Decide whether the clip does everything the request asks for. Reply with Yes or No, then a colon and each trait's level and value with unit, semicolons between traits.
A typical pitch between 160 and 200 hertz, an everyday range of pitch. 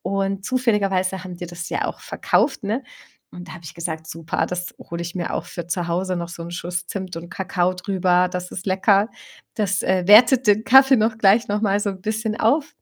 Yes: high, 190 Hz; average, 3.1 semitones